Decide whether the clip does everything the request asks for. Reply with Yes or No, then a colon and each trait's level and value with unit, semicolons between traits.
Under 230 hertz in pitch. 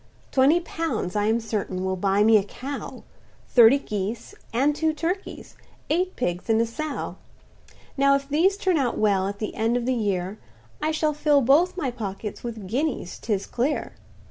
No: high, 240 Hz